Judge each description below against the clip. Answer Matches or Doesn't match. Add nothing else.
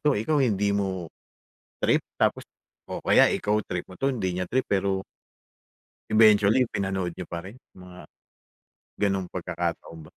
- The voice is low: Matches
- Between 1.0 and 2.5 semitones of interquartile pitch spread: Doesn't match